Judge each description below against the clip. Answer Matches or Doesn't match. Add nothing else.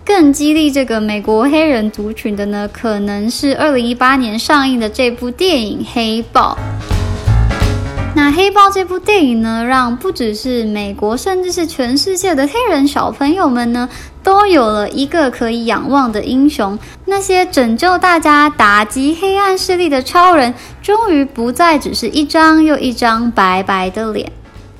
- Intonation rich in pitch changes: Matches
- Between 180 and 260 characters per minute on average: Matches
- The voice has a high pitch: Matches